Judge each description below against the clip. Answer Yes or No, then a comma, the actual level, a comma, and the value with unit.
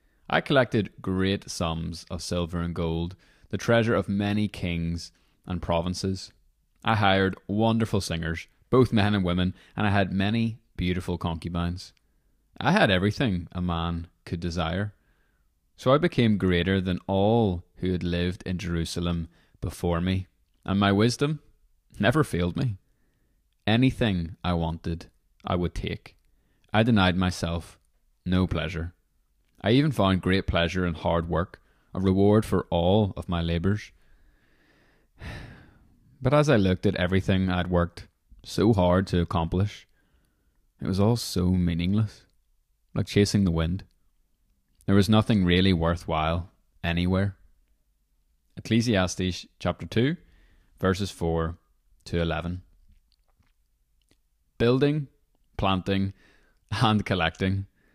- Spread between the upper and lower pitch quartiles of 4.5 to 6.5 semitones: No, average, 3.2 semitones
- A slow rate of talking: Yes, slow, 125 wpm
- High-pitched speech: No, very low, 90 Hz